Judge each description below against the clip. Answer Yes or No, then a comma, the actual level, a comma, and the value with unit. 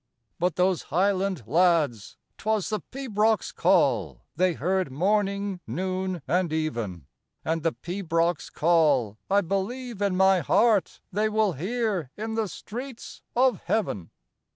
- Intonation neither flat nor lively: Yes, average, 4.3 semitones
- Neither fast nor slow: No, slow, 130 wpm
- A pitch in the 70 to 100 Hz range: No, medium, 185 Hz